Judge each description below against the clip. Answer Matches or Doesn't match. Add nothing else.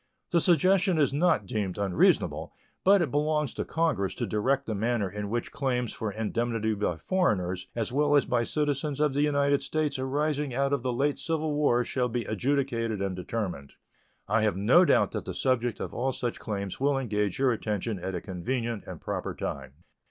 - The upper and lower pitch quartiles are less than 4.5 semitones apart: Doesn't match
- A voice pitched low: Matches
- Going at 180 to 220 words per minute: Matches